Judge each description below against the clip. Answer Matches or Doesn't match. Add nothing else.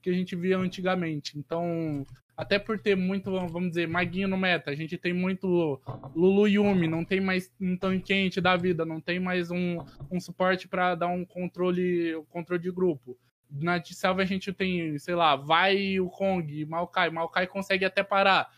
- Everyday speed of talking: Doesn't match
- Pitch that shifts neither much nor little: Doesn't match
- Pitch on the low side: Doesn't match